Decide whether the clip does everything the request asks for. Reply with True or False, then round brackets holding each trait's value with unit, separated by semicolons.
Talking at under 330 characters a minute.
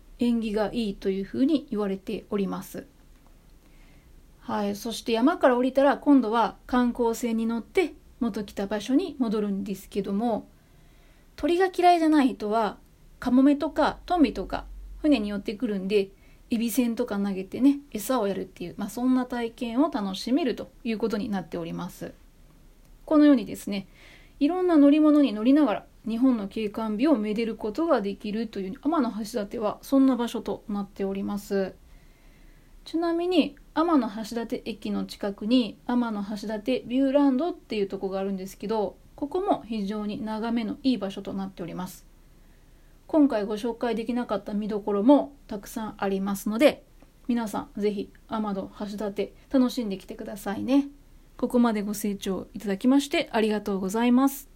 False (345 characters per minute)